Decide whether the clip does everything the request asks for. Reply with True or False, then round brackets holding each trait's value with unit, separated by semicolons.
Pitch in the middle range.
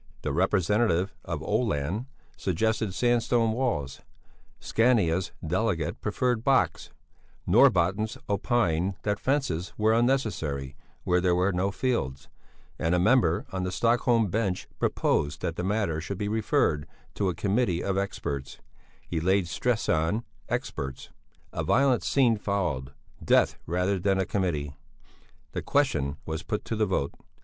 False (95 Hz)